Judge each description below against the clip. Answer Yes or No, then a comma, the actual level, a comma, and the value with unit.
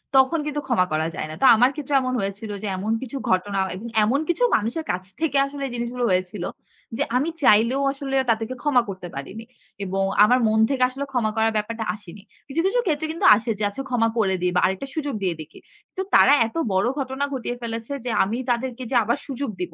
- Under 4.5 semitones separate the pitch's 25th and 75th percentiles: No, average, 5.0 semitones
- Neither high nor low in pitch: No, high, 235 Hz